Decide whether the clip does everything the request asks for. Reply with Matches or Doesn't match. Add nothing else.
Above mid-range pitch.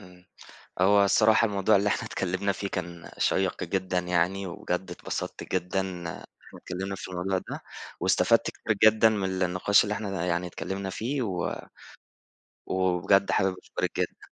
Doesn't match